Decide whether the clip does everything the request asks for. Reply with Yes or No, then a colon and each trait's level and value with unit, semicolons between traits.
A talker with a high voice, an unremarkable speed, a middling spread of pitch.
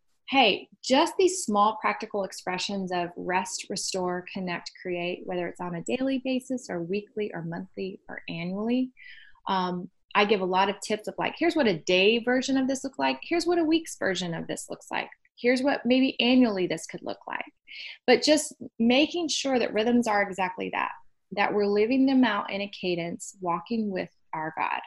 No: high, 210 Hz; average, 190 wpm; wide, 6.1 semitones